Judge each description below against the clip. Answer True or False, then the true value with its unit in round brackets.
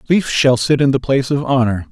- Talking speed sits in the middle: False (250 wpm)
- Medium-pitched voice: False (130 Hz)